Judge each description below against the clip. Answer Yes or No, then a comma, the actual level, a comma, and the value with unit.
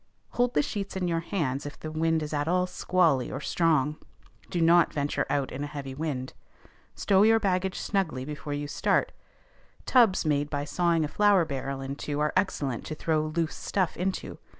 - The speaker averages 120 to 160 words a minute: No, average, 195 wpm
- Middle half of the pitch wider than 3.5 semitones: Yes, average, 4.0 semitones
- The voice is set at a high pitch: No, medium, 155 Hz